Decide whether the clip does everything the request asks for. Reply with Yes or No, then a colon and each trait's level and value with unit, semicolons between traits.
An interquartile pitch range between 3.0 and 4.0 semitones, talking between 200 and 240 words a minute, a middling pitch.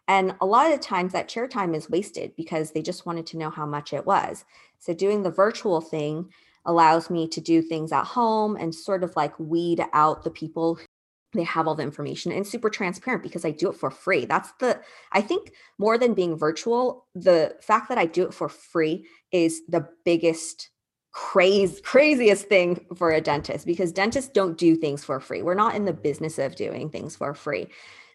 Yes: average, 3.7 semitones; fast, 205 wpm; medium, 170 Hz